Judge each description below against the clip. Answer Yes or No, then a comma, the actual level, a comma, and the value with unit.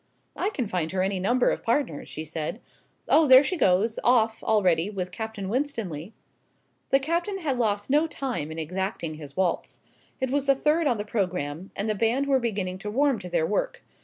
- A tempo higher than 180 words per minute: Yes, average, 195 wpm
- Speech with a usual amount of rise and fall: No, wide, 6.7 semitones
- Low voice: No, high, 215 Hz